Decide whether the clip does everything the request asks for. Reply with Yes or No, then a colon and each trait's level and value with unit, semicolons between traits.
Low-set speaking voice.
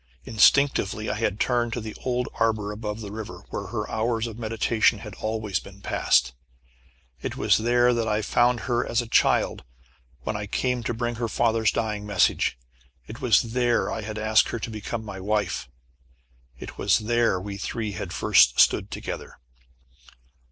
Yes: low, 110 Hz